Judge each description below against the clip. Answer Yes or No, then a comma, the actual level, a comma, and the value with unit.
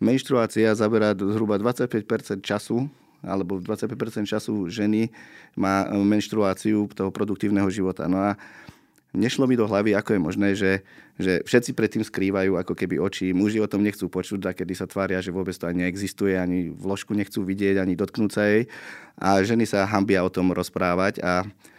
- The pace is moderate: No, fast, 170 wpm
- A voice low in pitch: Yes, low, 100 Hz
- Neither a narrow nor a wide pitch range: No, narrow, 2.0 semitones